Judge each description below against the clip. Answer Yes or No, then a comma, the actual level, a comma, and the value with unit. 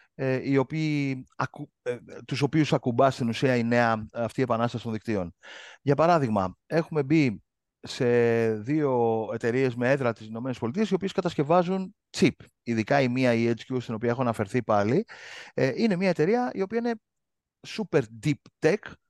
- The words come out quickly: No, average, 145 wpm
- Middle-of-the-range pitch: No, low, 130 Hz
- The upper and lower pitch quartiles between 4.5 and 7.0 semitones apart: Yes, average, 5.2 semitones